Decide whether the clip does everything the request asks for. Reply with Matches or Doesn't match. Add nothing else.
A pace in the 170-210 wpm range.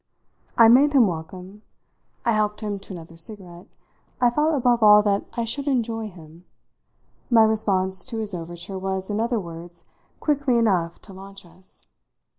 Doesn't match